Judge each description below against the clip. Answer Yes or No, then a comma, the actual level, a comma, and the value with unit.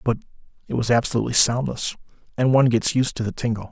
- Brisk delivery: No, average, 195 wpm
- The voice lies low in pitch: Yes, low, 120 Hz